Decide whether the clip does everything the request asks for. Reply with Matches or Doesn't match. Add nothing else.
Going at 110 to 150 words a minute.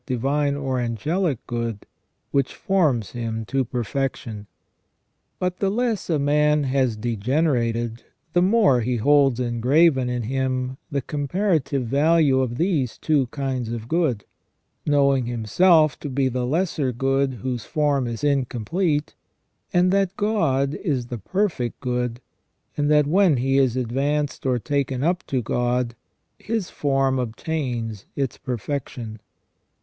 Matches